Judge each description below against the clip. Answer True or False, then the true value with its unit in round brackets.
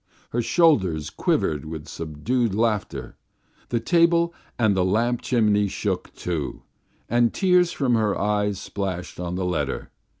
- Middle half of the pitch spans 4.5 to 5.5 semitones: True (5.2 semitones)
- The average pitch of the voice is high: False (105 Hz)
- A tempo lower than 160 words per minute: True (135 wpm)